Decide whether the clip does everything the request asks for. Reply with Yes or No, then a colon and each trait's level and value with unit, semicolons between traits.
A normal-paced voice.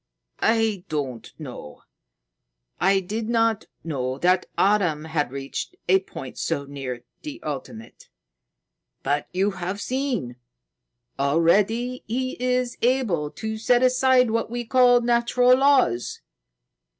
No: slow, 115 wpm